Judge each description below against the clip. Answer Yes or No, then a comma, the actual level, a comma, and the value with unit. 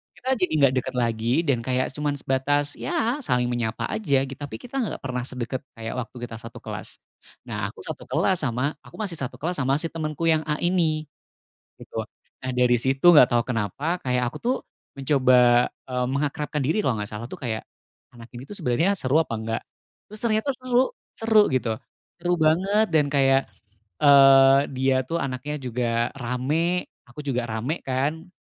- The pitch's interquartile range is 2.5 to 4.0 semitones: No, average, 4.7 semitones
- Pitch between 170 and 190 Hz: No, low, 135 Hz